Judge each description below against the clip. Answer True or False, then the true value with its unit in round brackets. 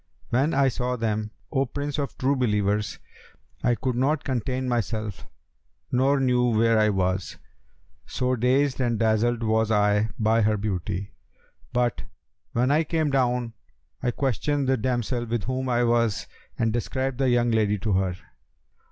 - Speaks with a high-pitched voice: False (120 Hz)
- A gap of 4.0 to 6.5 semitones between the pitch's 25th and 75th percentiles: False (3.2 semitones)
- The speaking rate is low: False (150 wpm)